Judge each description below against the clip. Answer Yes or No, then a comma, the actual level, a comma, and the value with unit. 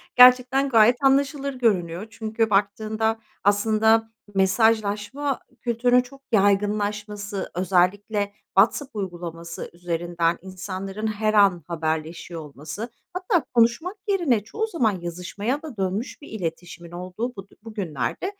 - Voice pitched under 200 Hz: No, high, 210 Hz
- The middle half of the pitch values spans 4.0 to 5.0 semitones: Yes, average, 4.5 semitones